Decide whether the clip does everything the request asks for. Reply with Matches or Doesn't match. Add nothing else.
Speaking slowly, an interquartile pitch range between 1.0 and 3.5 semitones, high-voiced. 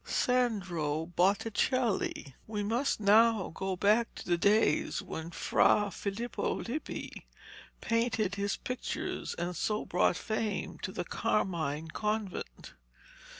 Doesn't match